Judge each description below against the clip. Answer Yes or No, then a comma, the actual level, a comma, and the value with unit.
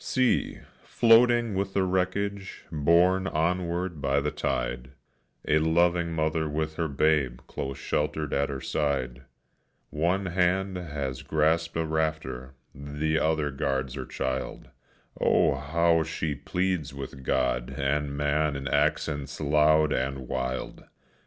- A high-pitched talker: No, very low, 75 Hz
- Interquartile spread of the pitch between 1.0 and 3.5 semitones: No, average, 3.9 semitones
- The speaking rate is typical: No, slow, 125 wpm